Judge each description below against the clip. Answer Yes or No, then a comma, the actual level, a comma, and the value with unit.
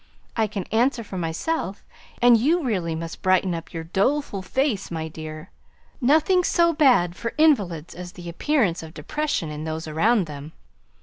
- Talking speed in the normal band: Yes, average, 165 wpm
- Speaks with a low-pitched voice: No, high, 190 Hz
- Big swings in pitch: Yes, wide, 8.0 semitones